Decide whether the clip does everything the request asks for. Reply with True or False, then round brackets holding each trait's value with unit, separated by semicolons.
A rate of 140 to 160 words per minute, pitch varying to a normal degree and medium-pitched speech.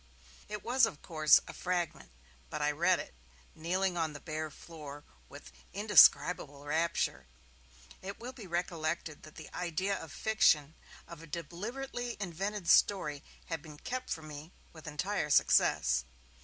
True (145 wpm; 4.2 semitones; 165 Hz)